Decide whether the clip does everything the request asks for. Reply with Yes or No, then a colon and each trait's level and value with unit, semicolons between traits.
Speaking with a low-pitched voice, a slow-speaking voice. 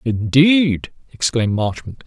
Yes: low, 130 Hz; slow, 85 wpm